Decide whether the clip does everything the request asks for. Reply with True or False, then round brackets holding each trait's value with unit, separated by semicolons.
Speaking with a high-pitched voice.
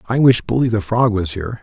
False (110 Hz)